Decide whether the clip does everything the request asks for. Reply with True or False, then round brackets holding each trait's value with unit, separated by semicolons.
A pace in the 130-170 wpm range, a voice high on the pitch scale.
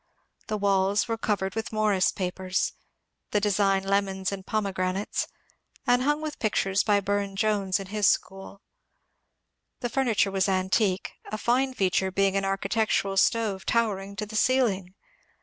True (155 wpm; 200 Hz)